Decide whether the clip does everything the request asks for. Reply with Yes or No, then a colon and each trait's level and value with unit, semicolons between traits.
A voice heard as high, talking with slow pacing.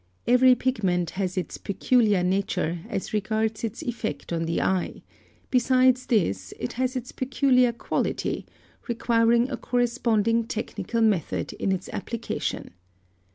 Yes: high, 225 Hz; slow, 125 wpm